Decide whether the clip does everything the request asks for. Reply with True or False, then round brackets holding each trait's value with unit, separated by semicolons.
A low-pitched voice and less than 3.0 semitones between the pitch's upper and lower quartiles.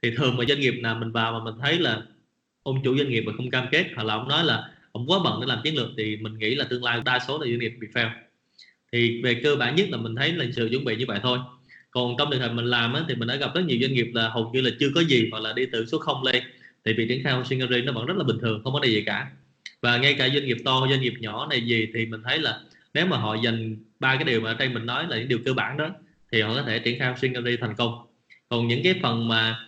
True (120 Hz; 2.5 semitones)